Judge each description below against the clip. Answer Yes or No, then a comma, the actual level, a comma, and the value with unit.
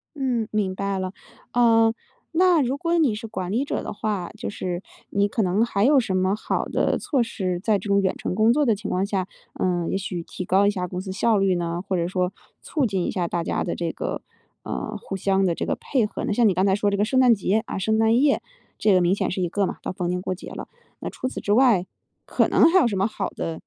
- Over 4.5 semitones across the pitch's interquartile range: No, average, 3.6 semitones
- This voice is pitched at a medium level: No, high, 200 Hz